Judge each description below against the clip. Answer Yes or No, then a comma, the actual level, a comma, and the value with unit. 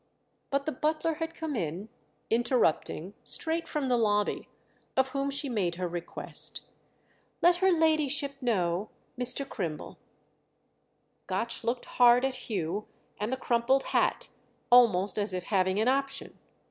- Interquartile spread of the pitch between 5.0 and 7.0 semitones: Yes, wide, 5.6 semitones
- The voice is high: Yes, high, 245 Hz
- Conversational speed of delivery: No, slow, 130 wpm